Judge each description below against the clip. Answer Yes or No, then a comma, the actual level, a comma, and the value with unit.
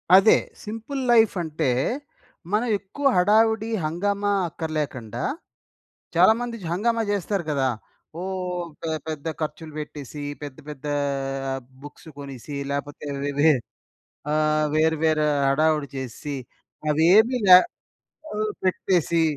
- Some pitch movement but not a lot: No, wide, 5.8 semitones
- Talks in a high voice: No, medium, 160 Hz